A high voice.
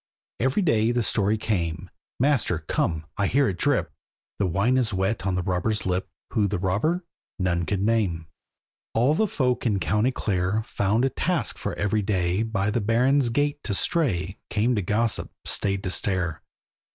No: low, 105 Hz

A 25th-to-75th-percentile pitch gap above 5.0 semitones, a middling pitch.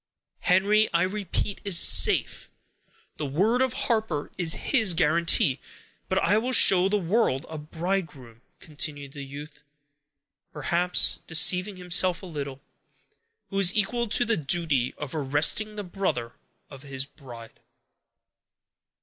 Yes: wide, 5.5 semitones; medium, 170 Hz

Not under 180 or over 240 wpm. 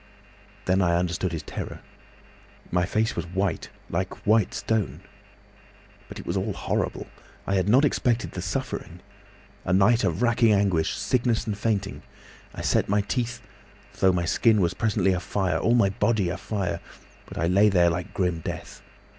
No: average, 160 wpm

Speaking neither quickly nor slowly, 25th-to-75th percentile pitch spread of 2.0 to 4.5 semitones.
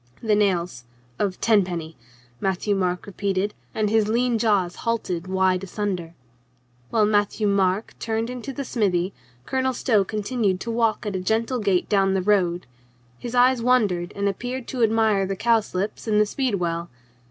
Yes: average, 165 wpm; average, 3.4 semitones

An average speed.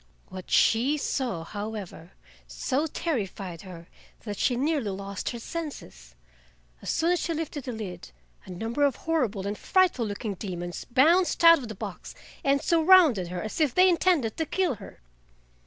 Yes: average, 165 wpm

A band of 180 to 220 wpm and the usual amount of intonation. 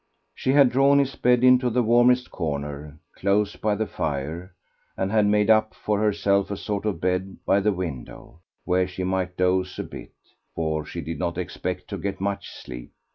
Yes: average, 185 wpm; average, 3.2 semitones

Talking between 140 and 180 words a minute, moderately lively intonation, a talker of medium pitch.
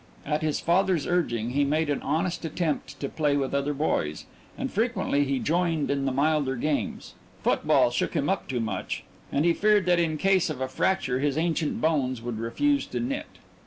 No: average, 195 wpm; average, 4.1 semitones; medium, 150 Hz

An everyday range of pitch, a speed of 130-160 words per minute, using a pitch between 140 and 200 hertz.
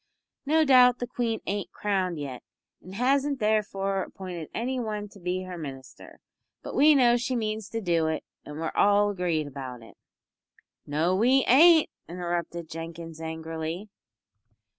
No: wide, 6.4 semitones; average, 150 wpm; high, 190 Hz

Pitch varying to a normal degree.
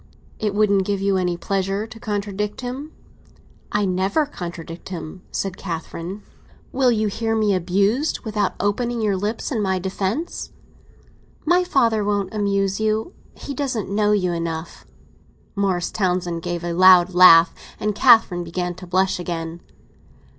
Yes: average, 3.3 semitones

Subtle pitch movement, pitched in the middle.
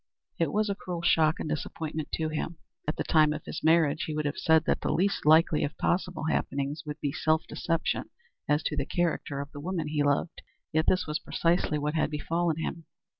Yes: narrow, 1.9 semitones; medium, 155 Hz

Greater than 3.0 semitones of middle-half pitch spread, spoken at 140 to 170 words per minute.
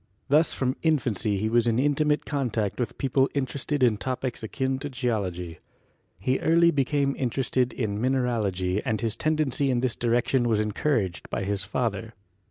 Yes: average, 4.0 semitones; average, 165 wpm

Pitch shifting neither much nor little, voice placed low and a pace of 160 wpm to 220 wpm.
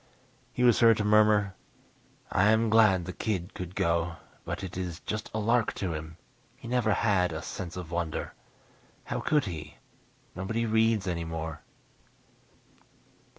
No: average, 4.6 semitones; very low, 95 Hz; average, 150 wpm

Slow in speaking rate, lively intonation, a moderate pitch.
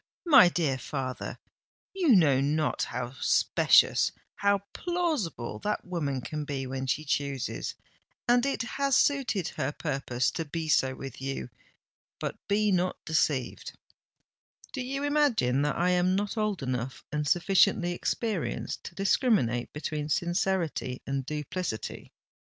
Yes: slow, 130 wpm; wide, 7.2 semitones; medium, 165 Hz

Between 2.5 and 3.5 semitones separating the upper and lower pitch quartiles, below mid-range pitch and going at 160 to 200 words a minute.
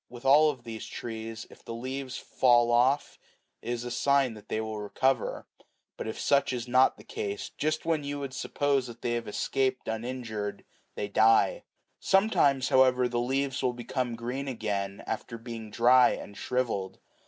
Yes: average, 2.9 semitones; low, 125 Hz; average, 175 wpm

